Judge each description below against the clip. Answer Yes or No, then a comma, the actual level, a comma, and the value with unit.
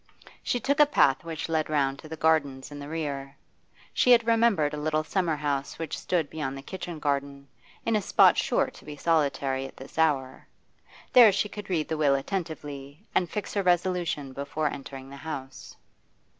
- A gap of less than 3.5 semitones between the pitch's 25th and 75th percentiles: No, average, 4.1 semitones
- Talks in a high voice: No, medium, 155 Hz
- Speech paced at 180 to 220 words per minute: Yes, average, 185 wpm